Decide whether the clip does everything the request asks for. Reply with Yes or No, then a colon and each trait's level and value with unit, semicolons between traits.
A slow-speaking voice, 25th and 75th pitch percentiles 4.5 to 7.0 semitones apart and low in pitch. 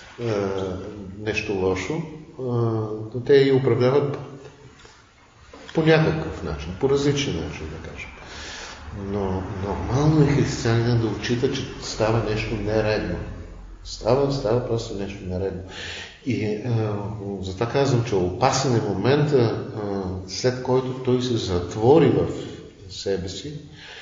Yes: slow, 110 wpm; average, 5.2 semitones; low, 110 Hz